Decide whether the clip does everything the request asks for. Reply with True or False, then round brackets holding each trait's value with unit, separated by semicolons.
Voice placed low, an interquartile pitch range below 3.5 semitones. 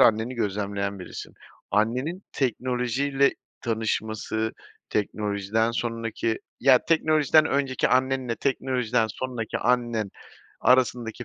True (120 Hz; 2.9 semitones)